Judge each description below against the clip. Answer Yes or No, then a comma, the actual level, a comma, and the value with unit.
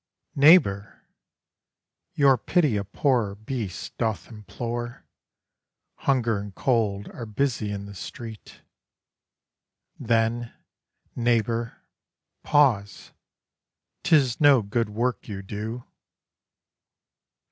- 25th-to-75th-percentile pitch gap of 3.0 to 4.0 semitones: Yes, average, 3.4 semitones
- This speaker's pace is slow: Yes, slow, 85 wpm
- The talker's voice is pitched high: No, low, 115 Hz